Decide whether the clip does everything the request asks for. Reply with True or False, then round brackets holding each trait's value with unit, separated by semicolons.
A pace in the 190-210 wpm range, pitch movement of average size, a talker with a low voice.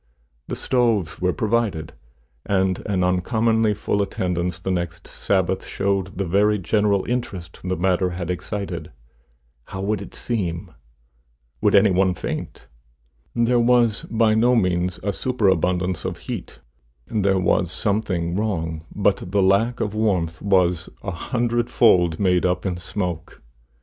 False (140 wpm; 3.3 semitones; 95 Hz)